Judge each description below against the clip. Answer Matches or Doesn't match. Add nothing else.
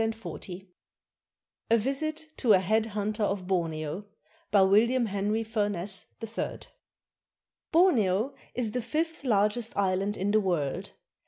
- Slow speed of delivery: Matches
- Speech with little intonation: Doesn't match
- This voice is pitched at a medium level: Doesn't match